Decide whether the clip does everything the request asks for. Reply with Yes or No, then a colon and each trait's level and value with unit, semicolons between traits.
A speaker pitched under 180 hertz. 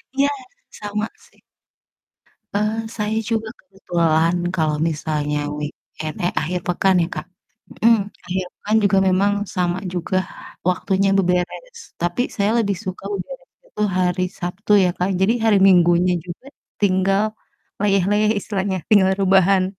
No: high, 190 Hz